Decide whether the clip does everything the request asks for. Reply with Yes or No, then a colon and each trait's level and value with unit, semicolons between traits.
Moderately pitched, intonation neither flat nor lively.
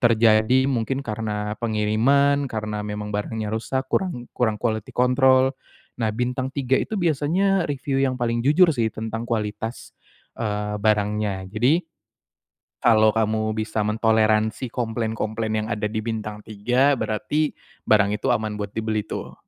No: low, 110 Hz; average, 3.3 semitones